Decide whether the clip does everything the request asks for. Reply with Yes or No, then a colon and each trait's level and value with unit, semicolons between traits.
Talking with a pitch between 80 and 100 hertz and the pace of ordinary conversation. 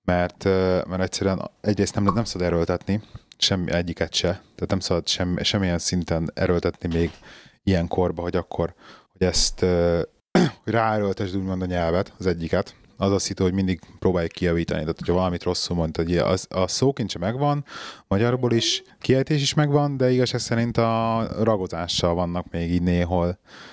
No: very low, 95 Hz; fast, 165 wpm